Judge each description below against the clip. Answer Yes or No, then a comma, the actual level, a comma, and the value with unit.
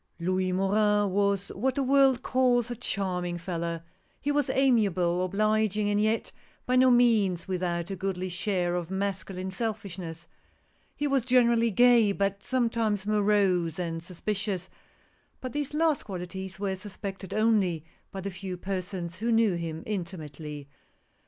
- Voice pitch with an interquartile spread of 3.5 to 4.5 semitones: Yes, average, 3.8 semitones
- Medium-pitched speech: No, high, 195 Hz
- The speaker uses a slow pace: No, average, 150 wpm